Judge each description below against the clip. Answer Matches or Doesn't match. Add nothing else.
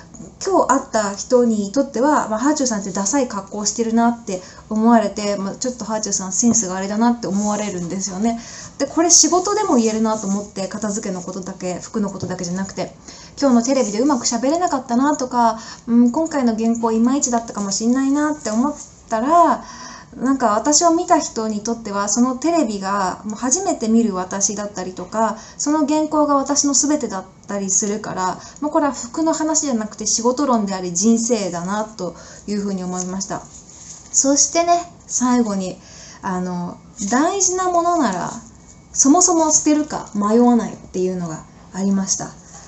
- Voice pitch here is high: Matches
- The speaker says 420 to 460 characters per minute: Doesn't match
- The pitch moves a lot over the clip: Matches